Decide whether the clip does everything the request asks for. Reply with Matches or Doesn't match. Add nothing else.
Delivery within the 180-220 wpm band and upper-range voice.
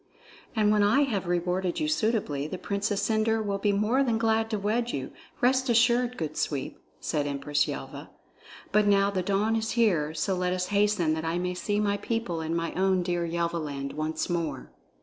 Matches